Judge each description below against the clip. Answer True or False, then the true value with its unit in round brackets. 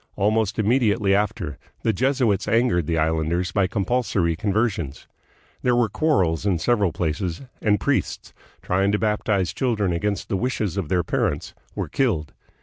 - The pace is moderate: True (145 wpm)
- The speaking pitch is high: False (100 Hz)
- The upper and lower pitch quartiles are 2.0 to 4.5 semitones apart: True (4.2 semitones)